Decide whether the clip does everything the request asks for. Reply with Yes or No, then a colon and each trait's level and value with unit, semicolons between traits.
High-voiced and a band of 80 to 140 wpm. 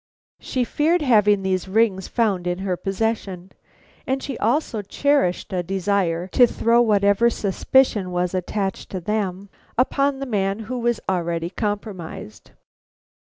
Yes: high, 200 Hz; slow, 135 wpm